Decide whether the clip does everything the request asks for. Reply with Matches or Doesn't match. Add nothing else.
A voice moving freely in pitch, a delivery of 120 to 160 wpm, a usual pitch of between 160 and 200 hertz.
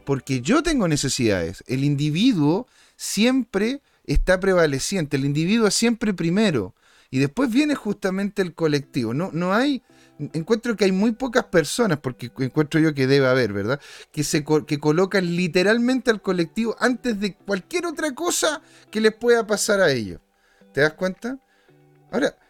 Matches